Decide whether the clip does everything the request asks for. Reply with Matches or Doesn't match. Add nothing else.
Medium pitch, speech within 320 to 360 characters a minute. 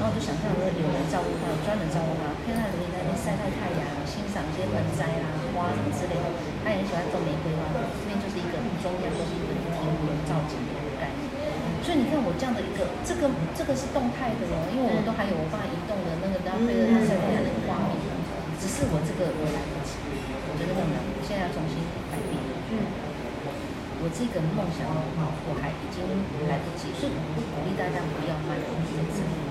Matches